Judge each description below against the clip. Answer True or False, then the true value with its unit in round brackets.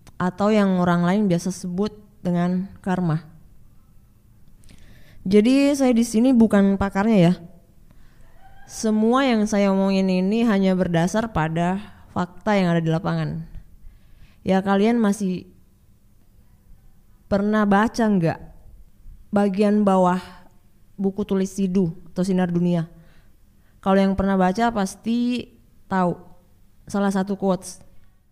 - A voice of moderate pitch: True (180 Hz)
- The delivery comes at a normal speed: True (110 wpm)